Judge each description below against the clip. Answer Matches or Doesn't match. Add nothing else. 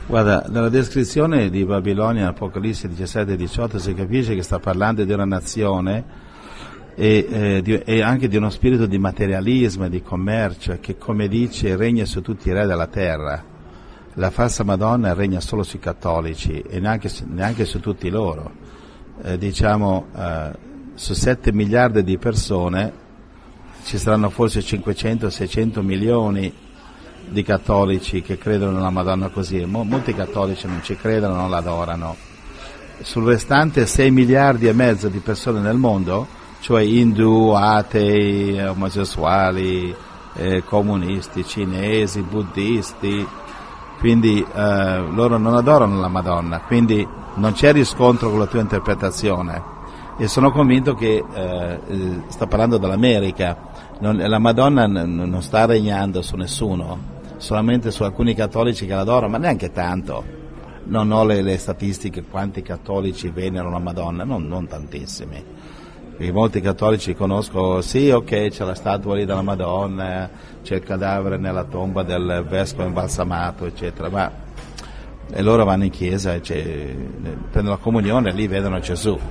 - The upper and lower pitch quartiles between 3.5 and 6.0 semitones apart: Doesn't match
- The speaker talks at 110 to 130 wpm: Doesn't match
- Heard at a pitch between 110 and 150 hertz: Doesn't match